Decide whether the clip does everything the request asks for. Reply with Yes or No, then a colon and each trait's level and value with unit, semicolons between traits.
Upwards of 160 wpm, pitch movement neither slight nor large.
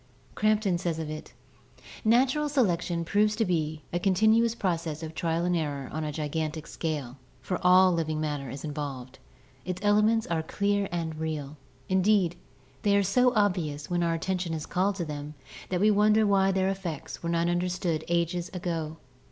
Yes: average, 175 wpm; average, 4.1 semitones